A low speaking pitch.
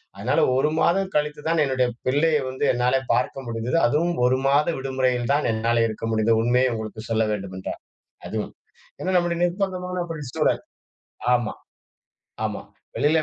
Yes: low, 130 Hz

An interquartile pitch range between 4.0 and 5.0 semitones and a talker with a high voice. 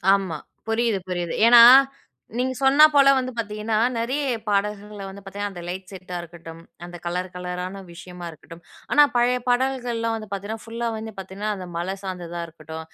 Yes: average, 4.3 semitones; high, 200 Hz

